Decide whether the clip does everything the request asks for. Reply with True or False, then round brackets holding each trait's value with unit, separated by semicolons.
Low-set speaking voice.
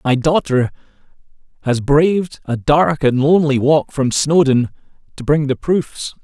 False (145 Hz)